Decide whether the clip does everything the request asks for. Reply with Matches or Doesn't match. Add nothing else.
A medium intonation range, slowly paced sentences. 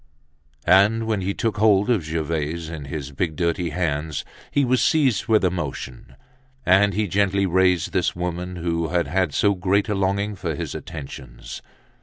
Doesn't match